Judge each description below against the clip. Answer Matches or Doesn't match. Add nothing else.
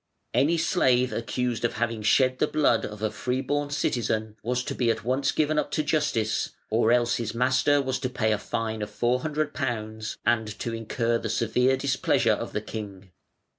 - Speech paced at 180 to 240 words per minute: Matches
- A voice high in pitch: Doesn't match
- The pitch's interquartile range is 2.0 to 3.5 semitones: Matches